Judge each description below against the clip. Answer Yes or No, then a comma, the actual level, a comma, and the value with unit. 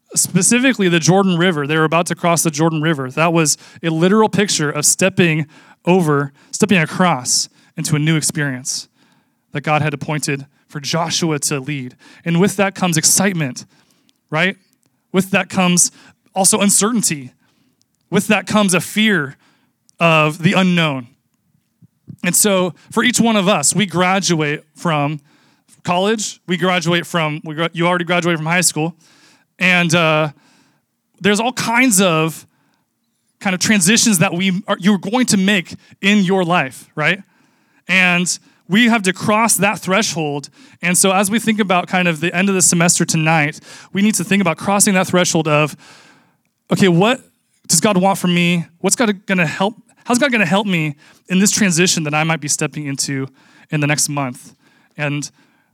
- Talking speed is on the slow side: No, average, 165 wpm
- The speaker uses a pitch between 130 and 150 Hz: No, medium, 180 Hz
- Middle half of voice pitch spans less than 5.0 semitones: Yes, average, 4.1 semitones